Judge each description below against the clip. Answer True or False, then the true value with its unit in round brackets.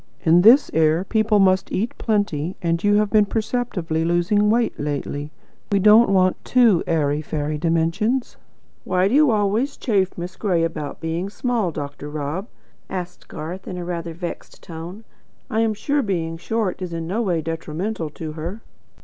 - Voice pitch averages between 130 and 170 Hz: False (180 Hz)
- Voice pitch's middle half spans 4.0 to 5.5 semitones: True (4.6 semitones)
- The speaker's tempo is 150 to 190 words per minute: True (165 wpm)